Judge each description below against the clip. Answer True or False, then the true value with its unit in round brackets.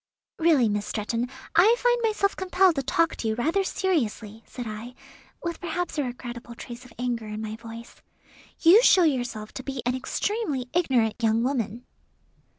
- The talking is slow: False (165 wpm)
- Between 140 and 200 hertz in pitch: False (250 Hz)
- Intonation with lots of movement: True (6.8 semitones)